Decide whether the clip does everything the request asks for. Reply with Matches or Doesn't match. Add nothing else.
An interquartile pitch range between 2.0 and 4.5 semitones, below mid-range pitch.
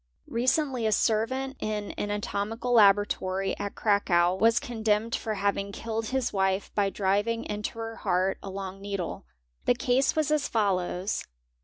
Doesn't match